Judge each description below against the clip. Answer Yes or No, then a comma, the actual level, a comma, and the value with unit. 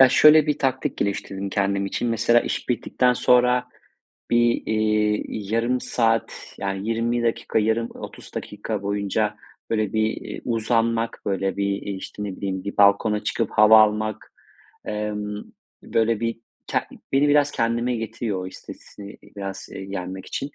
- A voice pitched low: Yes, low, 110 Hz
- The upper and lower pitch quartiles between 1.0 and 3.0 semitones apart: Yes, average, 2.7 semitones